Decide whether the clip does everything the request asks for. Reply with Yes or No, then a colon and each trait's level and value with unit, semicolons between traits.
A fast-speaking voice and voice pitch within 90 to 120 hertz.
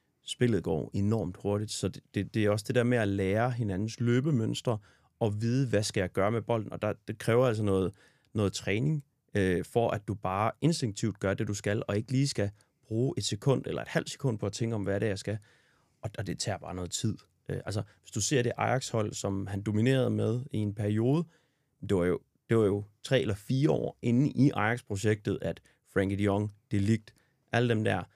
Yes: fast, 230 wpm; low, 110 Hz